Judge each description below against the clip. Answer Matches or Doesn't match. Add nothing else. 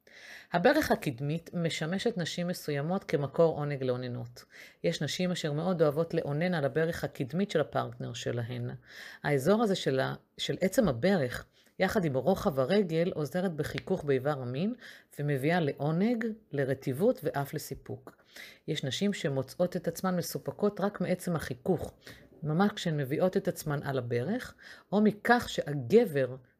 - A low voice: Doesn't match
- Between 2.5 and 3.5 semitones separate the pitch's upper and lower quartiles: Doesn't match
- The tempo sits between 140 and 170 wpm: Doesn't match